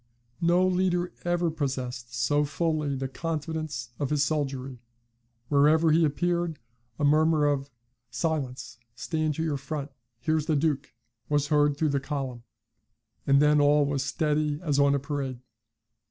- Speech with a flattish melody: Yes, narrow, 2.3 semitones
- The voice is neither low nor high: Yes, medium, 145 Hz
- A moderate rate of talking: Yes, average, 145 wpm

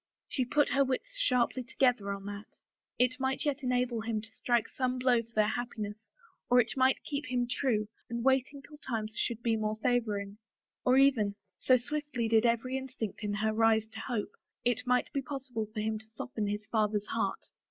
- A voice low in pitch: No, high, 240 Hz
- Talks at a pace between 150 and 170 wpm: No, average, 195 wpm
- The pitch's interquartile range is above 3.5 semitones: No, average, 3.0 semitones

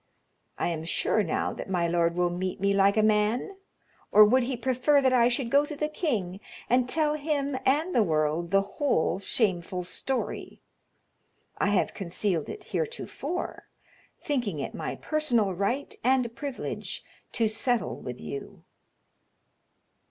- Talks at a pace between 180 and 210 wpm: No, average, 150 wpm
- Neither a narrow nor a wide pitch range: No, wide, 6.8 semitones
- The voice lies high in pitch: Yes, high, 225 Hz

